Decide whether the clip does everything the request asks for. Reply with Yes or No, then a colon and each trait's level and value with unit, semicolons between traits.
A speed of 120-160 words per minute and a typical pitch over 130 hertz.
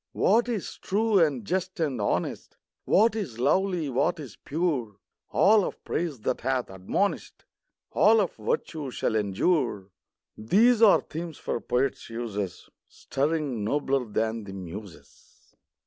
Yes: average, 140 wpm; medium, 140 Hz